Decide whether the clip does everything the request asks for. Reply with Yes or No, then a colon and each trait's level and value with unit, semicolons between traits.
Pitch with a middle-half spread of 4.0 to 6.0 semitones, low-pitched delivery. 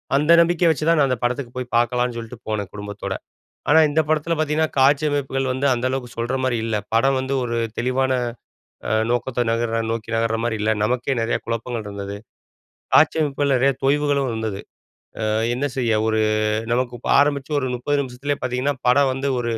No: average, 3.3 semitones; low, 125 Hz